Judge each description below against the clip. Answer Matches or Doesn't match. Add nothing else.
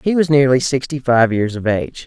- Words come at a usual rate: Doesn't match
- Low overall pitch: Matches